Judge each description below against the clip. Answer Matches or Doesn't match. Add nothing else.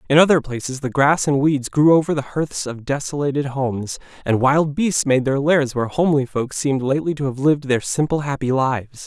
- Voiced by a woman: Doesn't match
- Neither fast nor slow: Doesn't match